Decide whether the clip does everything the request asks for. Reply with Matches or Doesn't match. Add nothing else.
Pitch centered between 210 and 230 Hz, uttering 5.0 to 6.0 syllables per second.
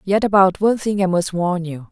Doesn't match